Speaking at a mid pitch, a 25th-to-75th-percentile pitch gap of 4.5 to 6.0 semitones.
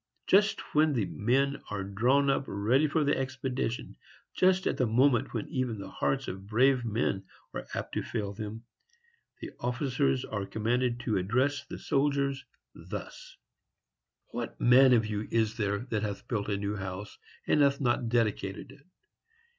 No: low, 120 Hz; average, 4.8 semitones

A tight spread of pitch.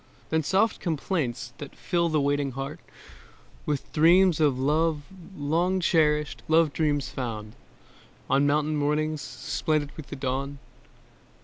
Yes: narrow, 2.3 semitones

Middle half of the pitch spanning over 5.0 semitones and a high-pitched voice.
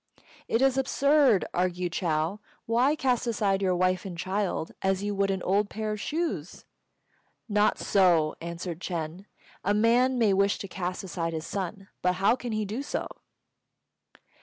No: average, 3.8 semitones; high, 195 Hz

